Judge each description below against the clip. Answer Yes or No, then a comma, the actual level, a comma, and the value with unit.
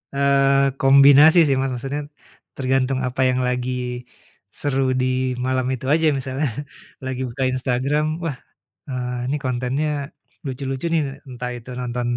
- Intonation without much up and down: Yes, narrow, 1.5 semitones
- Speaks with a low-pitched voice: Yes, low, 130 Hz